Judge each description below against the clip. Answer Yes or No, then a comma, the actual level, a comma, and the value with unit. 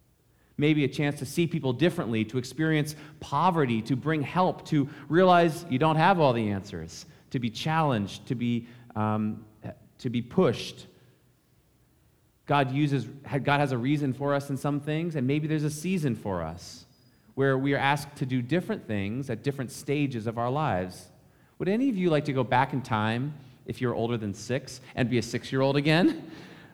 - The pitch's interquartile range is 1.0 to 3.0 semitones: No, average, 4.1 semitones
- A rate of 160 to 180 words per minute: No, average, 190 wpm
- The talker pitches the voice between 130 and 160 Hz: Yes, low, 135 Hz